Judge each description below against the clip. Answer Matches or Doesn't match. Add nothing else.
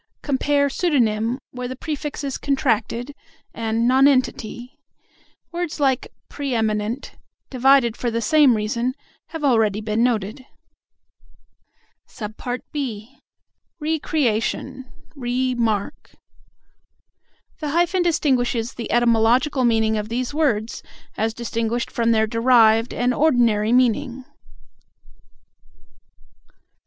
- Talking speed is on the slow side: Matches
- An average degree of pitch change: Matches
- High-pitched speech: Matches